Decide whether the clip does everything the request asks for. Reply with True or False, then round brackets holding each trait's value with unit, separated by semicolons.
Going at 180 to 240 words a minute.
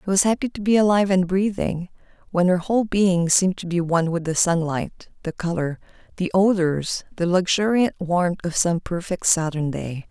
True (185 wpm)